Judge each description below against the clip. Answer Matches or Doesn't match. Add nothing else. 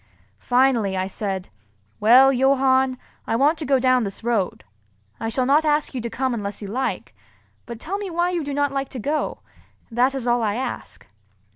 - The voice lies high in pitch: Matches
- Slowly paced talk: Doesn't match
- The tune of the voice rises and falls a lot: Doesn't match